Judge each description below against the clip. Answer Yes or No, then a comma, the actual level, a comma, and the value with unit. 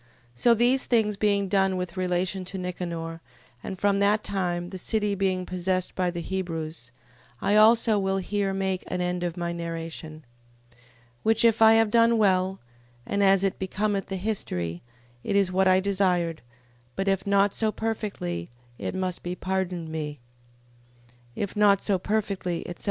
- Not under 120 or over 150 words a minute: No, average, 165 wpm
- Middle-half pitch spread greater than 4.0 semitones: No, narrow, 2.4 semitones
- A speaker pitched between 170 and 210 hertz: Yes, high, 190 Hz